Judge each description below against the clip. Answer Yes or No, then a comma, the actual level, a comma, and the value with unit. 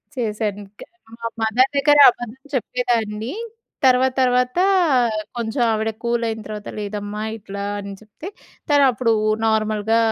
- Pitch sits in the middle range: No, high, 225 Hz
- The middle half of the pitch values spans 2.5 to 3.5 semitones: Yes, average, 2.8 semitones